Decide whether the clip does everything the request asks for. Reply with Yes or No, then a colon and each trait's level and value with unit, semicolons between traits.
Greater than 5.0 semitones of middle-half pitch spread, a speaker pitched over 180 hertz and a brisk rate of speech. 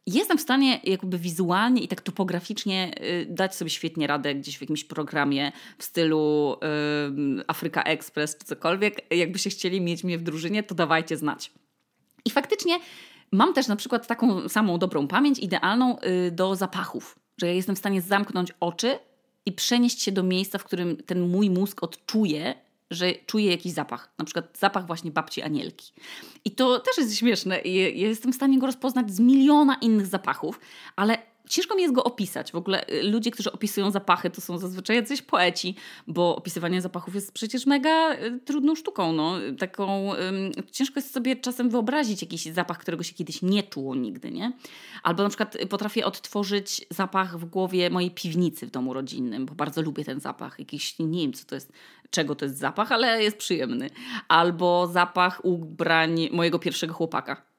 Yes: wide, 5.6 semitones; high, 190 Hz; fast, 175 wpm